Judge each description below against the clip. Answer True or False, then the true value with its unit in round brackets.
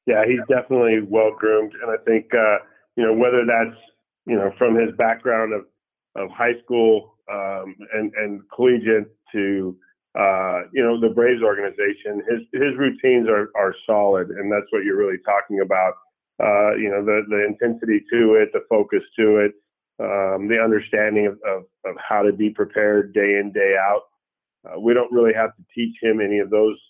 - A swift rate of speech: False (185 wpm)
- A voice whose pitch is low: True (110 Hz)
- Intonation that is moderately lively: False (2.3 semitones)